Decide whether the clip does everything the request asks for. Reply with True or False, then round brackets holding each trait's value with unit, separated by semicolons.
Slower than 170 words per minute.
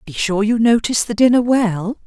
False (205 wpm)